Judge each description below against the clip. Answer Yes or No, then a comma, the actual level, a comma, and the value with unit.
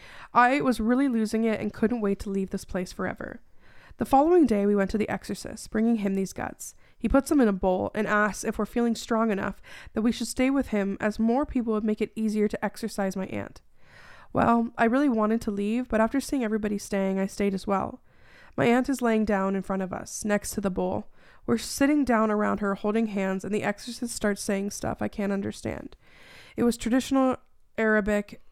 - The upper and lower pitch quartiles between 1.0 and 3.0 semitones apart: Yes, average, 2.7 semitones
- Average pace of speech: No, fast, 215 wpm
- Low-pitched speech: No, high, 215 Hz